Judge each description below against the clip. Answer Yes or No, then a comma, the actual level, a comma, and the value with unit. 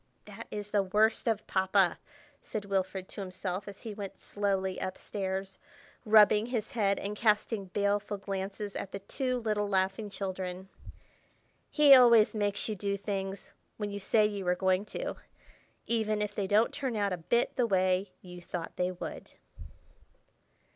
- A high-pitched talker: Yes, high, 200 Hz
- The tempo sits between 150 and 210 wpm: Yes, average, 155 wpm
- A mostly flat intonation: Yes, narrow, 1.9 semitones